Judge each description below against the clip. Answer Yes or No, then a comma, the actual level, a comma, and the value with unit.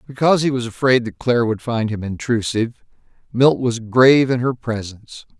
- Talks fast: No, average, 180 wpm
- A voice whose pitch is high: No, low, 120 Hz